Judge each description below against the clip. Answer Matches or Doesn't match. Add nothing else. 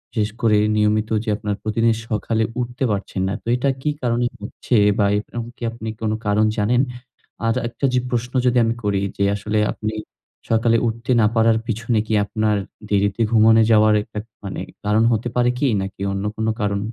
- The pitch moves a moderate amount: Doesn't match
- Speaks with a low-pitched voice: Matches